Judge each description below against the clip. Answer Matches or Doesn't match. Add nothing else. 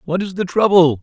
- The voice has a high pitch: Doesn't match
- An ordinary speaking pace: Doesn't match